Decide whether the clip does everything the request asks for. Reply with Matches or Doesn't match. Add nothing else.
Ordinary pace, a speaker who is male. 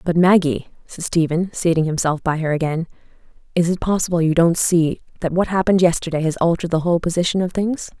Doesn't match